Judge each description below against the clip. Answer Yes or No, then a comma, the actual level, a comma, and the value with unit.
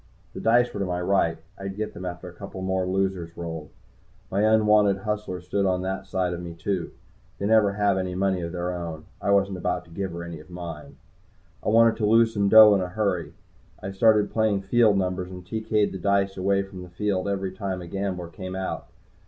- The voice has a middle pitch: No, very low, 95 Hz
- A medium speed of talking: No, fast, 220 wpm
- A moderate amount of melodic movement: No, narrow, 2.2 semitones